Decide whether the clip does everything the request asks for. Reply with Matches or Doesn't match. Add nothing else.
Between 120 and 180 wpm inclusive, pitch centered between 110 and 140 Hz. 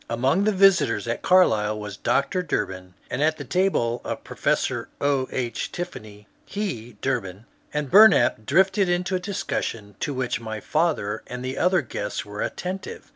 Matches